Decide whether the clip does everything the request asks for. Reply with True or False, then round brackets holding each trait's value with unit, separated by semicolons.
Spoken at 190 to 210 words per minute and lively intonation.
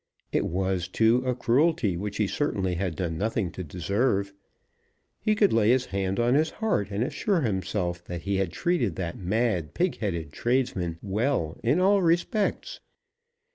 False (165 wpm; 6.2 semitones)